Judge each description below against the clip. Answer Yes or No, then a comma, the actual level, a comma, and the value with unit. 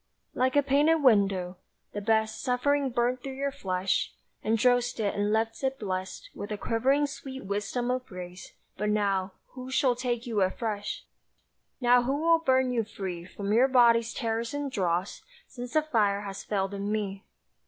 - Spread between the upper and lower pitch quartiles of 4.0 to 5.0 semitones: Yes, average, 4.4 semitones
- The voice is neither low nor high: No, high, 230 Hz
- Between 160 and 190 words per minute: Yes, average, 170 wpm